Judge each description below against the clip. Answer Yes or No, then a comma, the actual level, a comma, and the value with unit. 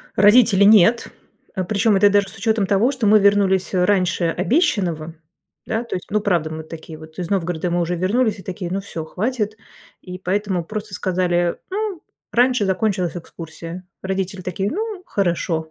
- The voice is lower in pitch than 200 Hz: Yes, high, 190 Hz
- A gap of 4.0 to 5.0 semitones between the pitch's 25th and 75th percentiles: No, average, 3.3 semitones